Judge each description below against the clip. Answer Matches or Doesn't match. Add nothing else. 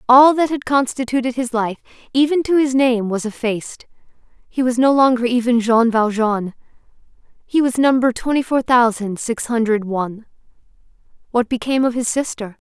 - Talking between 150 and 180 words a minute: Matches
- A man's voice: Doesn't match